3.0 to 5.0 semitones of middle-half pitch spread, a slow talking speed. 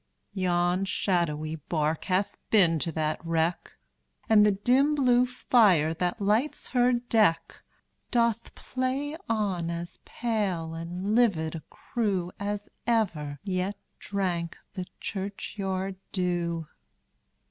Yes: average, 4.7 semitones; slow, 115 wpm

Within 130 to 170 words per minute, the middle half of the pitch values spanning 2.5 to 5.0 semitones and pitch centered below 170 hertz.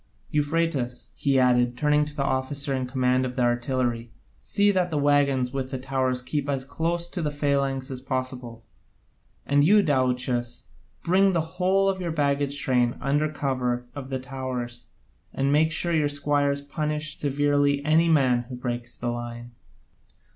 Yes: average, 160 wpm; average, 2.8 semitones; medium, 140 Hz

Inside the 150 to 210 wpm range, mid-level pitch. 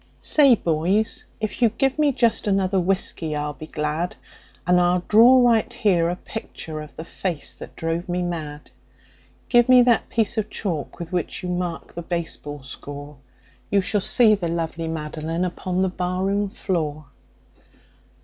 Yes: average, 160 wpm; medium, 180 Hz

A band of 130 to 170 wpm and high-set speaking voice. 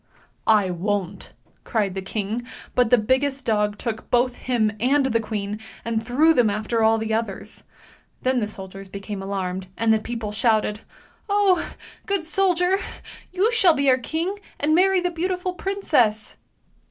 Yes: average, 165 wpm; high, 230 Hz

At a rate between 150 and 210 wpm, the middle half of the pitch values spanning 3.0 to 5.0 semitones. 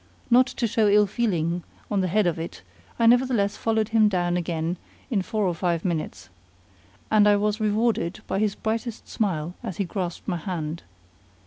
Yes: average, 180 wpm; average, 4.0 semitones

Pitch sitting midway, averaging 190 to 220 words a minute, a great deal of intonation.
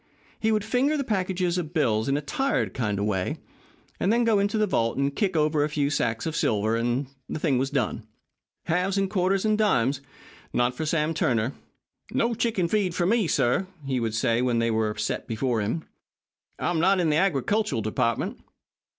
Yes: medium, 155 Hz; average, 195 wpm; wide, 8.7 semitones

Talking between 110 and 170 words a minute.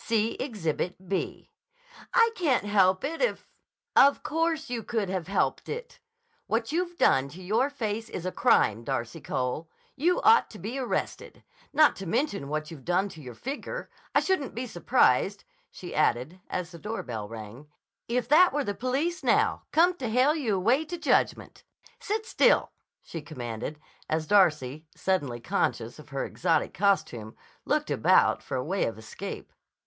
Yes: average, 165 wpm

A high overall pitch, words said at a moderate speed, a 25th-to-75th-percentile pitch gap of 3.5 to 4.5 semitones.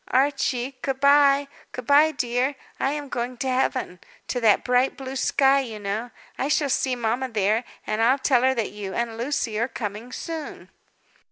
No: very high, 255 Hz; average, 180 wpm; average, 3.1 semitones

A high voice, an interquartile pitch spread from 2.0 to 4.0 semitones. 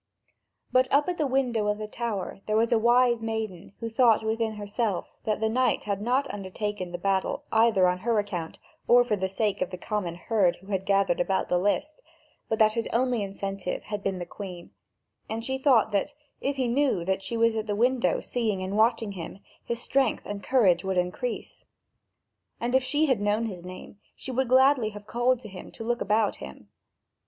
Yes: high, 215 Hz; average, 3.6 semitones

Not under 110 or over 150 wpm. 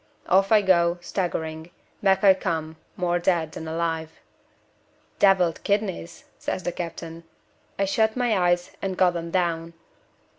Yes: average, 140 wpm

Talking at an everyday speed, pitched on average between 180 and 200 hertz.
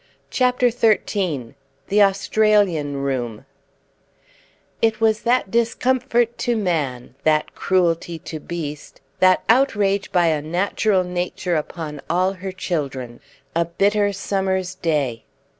No: slow, 110 wpm; medium, 185 Hz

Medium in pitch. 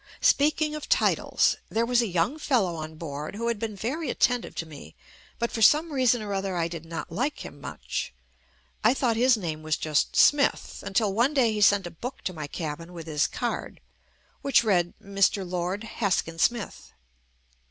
No: high, 200 Hz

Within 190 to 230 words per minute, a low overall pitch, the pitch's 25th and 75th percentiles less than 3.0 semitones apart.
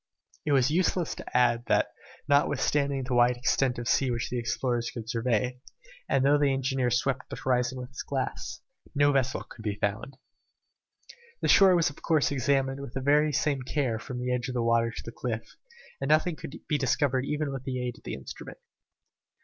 Yes: average, 195 wpm; low, 130 Hz; narrow, 2.6 semitones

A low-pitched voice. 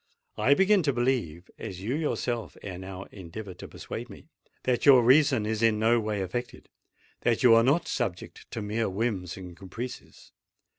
Yes: low, 115 Hz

